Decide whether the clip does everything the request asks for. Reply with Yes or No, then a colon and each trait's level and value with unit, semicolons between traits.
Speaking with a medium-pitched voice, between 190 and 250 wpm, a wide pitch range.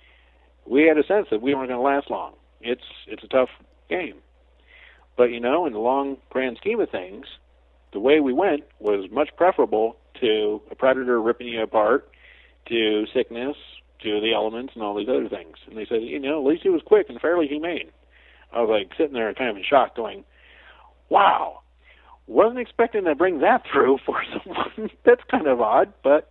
No: low, 120 Hz; average, 195 wpm; wide, 5.9 semitones